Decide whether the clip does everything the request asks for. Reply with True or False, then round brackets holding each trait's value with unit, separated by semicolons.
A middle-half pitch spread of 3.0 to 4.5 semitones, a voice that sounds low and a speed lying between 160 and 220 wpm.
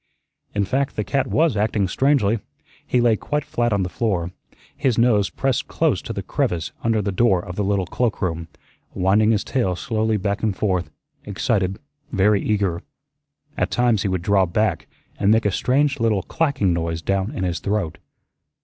True (3.8 semitones; 105 Hz; 175 wpm)